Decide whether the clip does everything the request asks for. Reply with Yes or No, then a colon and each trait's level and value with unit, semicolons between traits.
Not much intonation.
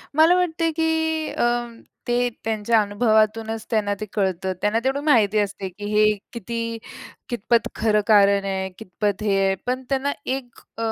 No: average, 4.1 semitones